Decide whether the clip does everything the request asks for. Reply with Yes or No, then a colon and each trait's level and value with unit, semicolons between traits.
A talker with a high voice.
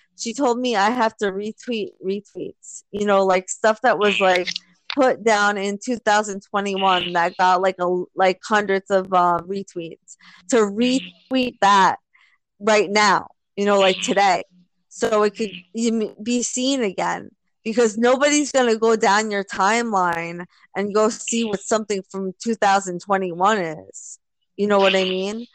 Yes: high, 200 Hz